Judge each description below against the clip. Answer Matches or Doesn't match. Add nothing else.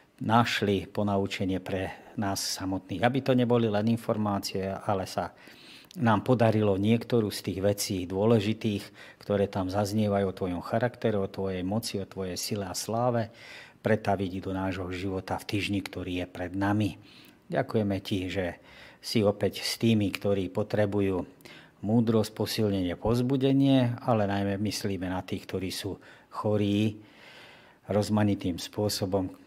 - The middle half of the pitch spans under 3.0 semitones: Matches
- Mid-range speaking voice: Doesn't match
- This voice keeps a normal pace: Matches